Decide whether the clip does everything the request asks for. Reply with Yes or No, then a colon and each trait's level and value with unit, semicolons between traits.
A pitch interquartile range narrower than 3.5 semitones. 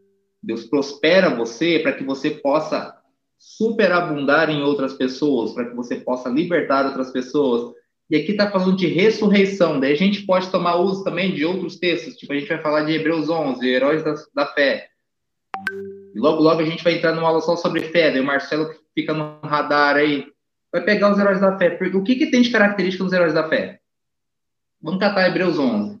No: average, 4.3 semitones